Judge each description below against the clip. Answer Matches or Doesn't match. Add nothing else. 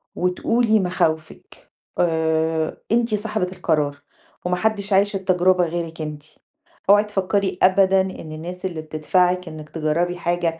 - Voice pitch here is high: Doesn't match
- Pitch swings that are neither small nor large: Matches